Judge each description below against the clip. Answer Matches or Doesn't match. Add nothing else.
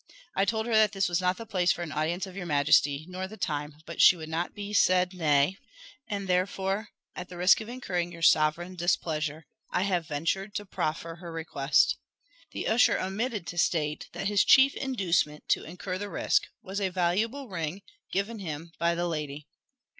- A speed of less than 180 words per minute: Doesn't match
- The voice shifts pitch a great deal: Doesn't match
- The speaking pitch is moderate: Matches